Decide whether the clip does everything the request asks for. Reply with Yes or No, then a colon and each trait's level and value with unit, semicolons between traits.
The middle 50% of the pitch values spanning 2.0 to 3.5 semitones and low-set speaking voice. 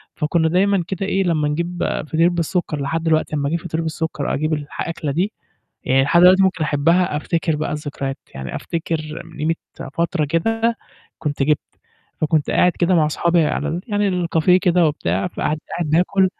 No: average, 2.8 semitones; medium, 165 Hz